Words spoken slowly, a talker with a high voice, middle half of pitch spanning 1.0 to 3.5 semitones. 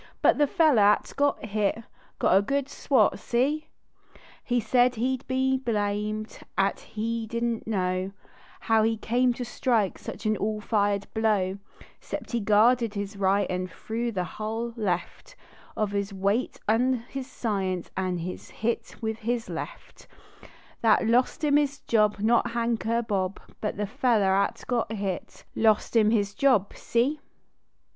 No: average, 155 wpm; high, 220 Hz; average, 3.0 semitones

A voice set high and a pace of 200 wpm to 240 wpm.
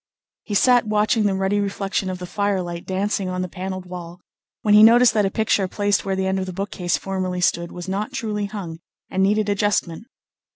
Yes: high, 195 Hz; fast, 205 wpm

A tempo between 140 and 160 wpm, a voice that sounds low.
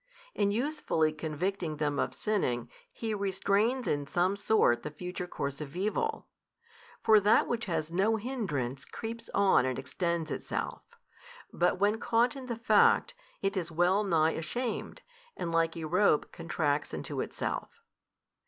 No: average, 145 wpm; medium, 185 Hz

